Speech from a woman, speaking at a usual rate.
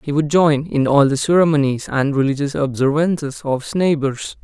No: male; average, 175 wpm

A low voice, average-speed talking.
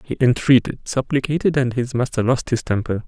Yes: low, 125 Hz; average, 155 wpm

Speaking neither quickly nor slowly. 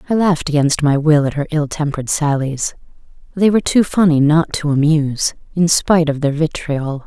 Yes: average, 185 wpm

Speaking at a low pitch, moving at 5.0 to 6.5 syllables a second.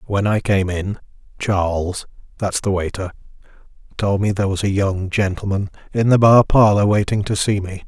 Yes: low, 100 Hz; 5.1 syllables/s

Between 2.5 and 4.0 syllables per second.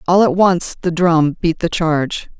No: 4.4 syllables/s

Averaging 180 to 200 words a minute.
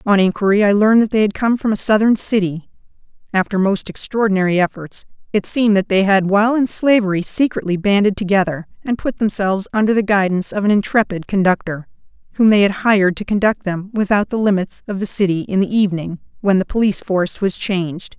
Yes: average, 195 wpm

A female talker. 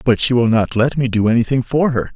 No: male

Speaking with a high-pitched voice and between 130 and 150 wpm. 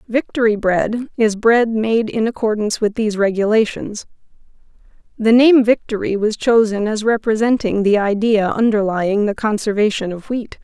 Yes: high, 215 Hz; slow, 135 wpm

